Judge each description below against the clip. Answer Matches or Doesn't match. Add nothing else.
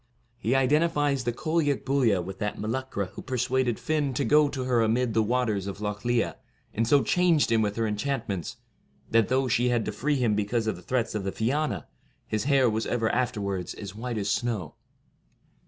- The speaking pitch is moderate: Doesn't match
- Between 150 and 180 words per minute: Doesn't match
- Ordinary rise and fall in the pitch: Matches